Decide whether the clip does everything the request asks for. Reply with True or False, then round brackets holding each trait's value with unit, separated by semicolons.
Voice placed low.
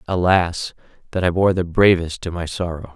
True (90 Hz)